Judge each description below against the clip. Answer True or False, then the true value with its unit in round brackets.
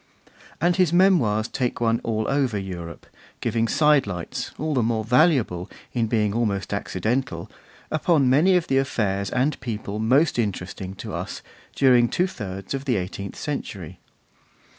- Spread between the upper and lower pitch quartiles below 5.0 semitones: False (5.5 semitones)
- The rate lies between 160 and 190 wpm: False (145 wpm)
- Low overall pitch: True (120 Hz)